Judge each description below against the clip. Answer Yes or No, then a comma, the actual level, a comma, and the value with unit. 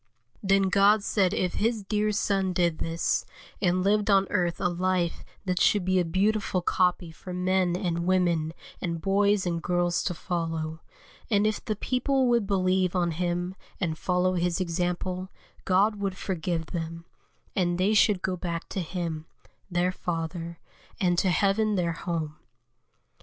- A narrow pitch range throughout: Yes, narrow, 2.3 semitones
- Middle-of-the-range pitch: Yes, medium, 180 Hz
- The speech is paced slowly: No, average, 160 wpm